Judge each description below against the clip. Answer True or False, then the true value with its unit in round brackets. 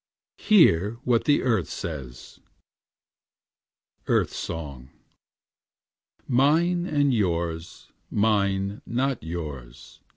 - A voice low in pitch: True (100 Hz)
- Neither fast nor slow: False (75 wpm)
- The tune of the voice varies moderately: False (8.4 semitones)